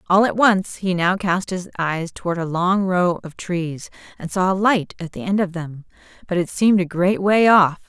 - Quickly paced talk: Yes, fast, 230 wpm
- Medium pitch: Yes, medium, 180 Hz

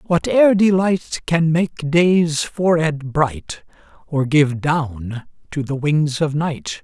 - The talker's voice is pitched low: No, medium, 155 Hz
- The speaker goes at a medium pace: No, slow, 130 wpm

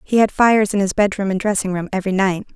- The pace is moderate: No, fast, 260 wpm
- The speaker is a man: No, female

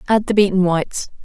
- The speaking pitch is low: No, high, 190 Hz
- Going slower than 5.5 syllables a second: No, 6.1 syllables/s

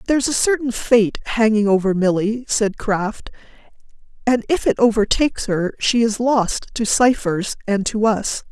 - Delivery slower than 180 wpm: Yes, average, 160 wpm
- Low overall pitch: No, high, 220 Hz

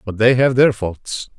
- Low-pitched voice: Yes, low, 115 Hz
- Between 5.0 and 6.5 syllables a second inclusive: No, 4.1 syllables/s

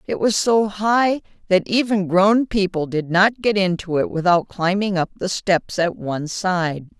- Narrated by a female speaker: Yes, female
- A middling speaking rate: Yes, average, 180 wpm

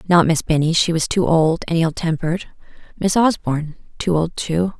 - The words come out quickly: No, average, 190 wpm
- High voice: No, medium, 170 Hz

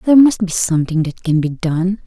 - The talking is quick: Yes, fast, 230 wpm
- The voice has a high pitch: No, medium, 180 Hz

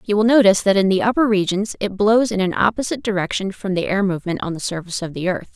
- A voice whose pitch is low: No, high, 200 Hz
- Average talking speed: No, fast, 260 wpm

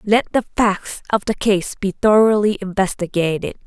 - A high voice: Yes, high, 200 Hz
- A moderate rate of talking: Yes, average, 145 wpm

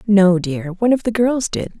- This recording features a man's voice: No, female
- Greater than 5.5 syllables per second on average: No, 5.0 syllables/s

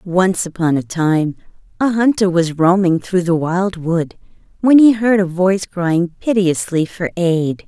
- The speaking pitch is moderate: Yes, medium, 180 Hz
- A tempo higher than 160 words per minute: No, average, 155 wpm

